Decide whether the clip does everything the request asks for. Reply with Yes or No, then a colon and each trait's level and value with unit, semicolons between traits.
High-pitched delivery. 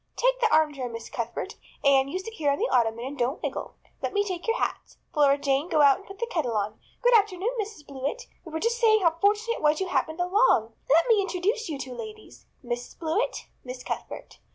Yes: very high, 330 Hz